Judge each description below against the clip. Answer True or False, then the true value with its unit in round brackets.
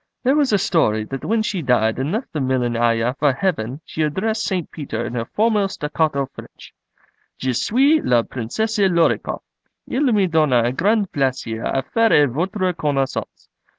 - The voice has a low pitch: False (150 Hz)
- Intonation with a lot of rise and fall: True (8.5 semitones)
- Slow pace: False (170 wpm)